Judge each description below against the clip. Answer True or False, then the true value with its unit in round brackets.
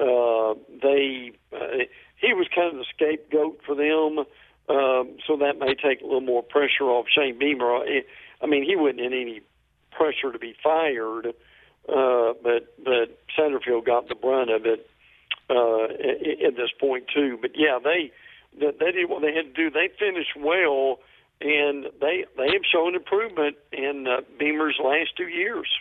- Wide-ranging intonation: True (8.9 semitones)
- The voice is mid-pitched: True (145 Hz)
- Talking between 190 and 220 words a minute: False (165 wpm)